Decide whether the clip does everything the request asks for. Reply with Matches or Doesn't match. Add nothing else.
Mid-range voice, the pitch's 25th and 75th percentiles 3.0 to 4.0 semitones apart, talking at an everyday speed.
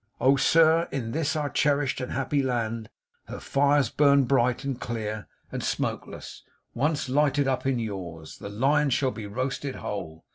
Doesn't match